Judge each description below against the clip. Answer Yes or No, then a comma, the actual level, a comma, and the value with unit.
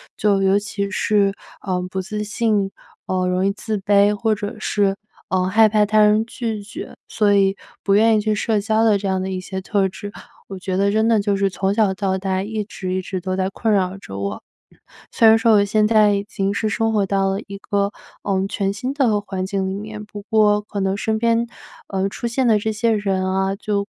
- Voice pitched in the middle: No, high, 200 Hz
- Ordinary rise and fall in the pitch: No, narrow, 1.9 semitones